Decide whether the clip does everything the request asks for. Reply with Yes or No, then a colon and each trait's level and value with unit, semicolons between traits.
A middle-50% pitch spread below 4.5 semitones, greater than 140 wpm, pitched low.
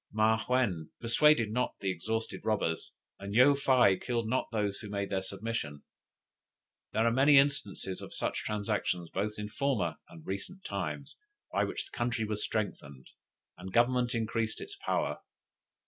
Yes: average, 3.8 semitones; average, 155 wpm; low, 110 Hz